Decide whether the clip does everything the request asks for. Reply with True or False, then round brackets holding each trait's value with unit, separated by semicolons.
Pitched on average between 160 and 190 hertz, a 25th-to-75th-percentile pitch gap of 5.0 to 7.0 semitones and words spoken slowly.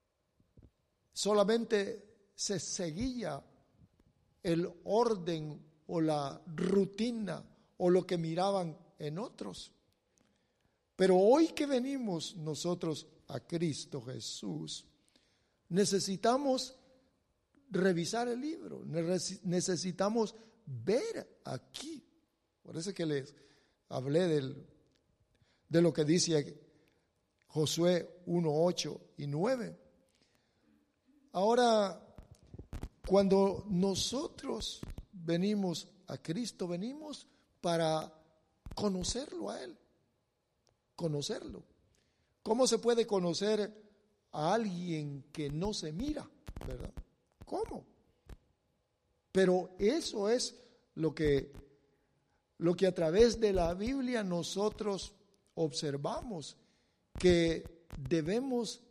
True (185 Hz; 5.5 semitones; 85 wpm)